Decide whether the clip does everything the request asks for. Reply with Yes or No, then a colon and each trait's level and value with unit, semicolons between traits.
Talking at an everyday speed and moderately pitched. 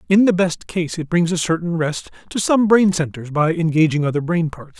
No: fast, 225 wpm; medium, 170 Hz